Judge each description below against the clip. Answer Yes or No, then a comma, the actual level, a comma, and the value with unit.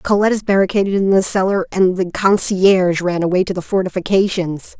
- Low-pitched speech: No, high, 190 Hz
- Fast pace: No, average, 175 wpm